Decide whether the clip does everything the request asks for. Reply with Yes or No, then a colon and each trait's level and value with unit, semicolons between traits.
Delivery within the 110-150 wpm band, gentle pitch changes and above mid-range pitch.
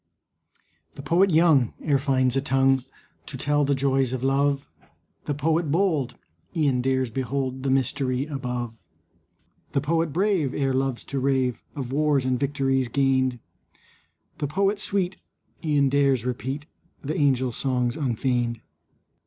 No: slow, 135 wpm; narrow, 2.2 semitones; low, 135 Hz